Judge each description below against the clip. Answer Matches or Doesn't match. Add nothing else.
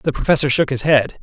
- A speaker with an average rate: Doesn't match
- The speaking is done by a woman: Doesn't match